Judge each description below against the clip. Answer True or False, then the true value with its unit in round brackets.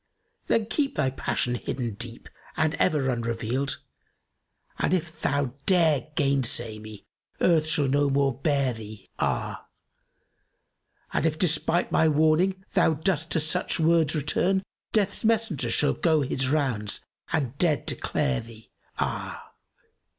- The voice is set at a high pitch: False (145 Hz)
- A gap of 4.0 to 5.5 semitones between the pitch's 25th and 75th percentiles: True (4.6 semitones)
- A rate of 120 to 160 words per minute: True (135 wpm)